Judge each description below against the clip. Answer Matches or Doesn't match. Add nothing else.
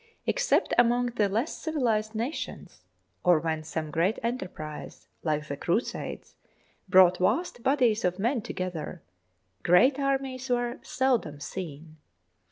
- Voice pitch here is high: Matches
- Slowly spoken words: Matches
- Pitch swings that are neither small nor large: Doesn't match